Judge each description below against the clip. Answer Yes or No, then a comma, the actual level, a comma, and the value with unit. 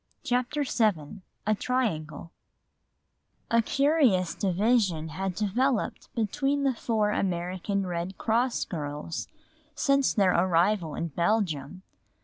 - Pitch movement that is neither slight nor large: No, wide, 5.8 semitones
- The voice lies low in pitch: No, high, 200 Hz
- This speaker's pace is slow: Yes, slow, 105 wpm